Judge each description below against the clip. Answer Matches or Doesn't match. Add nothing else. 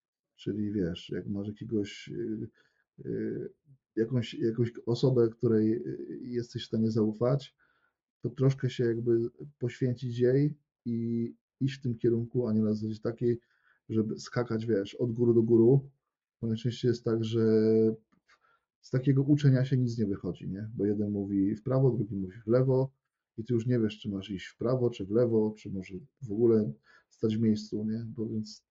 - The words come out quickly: Matches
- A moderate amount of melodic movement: Doesn't match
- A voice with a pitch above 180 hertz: Doesn't match